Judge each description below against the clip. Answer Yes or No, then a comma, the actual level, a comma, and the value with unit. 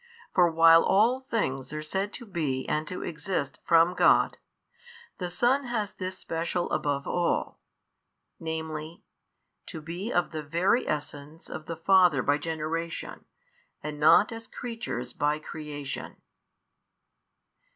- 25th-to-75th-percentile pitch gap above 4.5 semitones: No, average, 3.7 semitones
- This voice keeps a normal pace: No, slow, 130 wpm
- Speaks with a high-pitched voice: No, medium, 165 Hz